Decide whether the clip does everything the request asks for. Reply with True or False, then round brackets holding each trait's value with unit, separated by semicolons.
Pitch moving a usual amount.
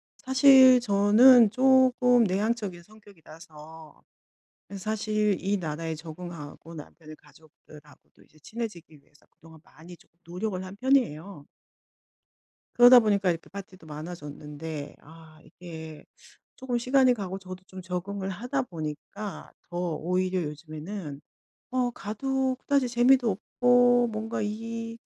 False (6.7 semitones)